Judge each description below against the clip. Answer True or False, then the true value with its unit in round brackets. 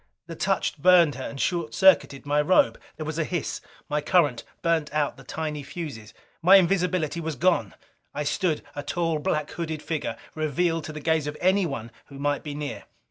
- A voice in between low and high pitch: True (155 Hz)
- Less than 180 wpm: False (185 wpm)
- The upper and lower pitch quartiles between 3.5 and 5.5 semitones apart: False (2.8 semitones)